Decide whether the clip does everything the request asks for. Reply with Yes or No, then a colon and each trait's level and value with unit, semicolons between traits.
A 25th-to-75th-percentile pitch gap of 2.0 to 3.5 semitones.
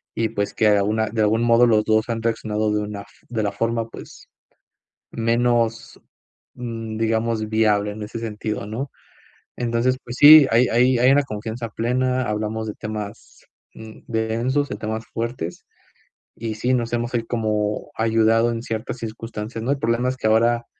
No: narrow, 1.5 semitones